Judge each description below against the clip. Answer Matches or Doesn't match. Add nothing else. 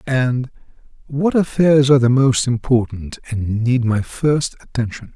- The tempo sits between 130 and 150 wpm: Matches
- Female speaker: Doesn't match